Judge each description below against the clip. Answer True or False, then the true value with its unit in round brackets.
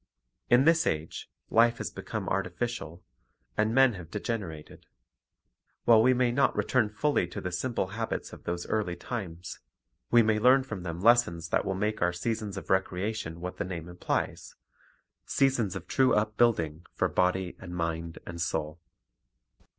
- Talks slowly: False (160 wpm)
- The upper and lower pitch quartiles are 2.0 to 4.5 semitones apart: False (5.2 semitones)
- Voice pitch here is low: True (95 Hz)